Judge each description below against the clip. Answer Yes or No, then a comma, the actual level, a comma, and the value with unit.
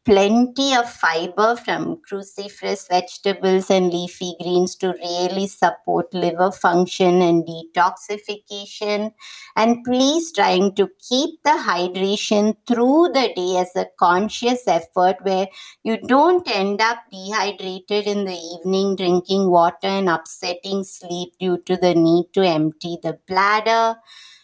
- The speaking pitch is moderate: No, high, 195 Hz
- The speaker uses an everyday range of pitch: Yes, average, 3.2 semitones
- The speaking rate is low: Yes, slow, 130 wpm